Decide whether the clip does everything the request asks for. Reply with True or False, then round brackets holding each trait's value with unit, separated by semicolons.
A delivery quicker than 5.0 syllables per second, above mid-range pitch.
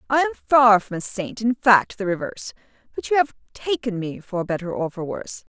True (5.3 syllables/s; 220 Hz)